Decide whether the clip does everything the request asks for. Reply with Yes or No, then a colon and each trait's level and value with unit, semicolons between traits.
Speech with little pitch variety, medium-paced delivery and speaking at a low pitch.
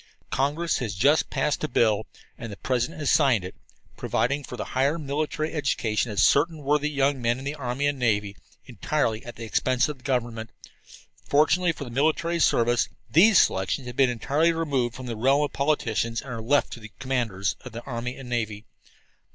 No: average, 4.0 semitones; average, 190 wpm; low, 130 Hz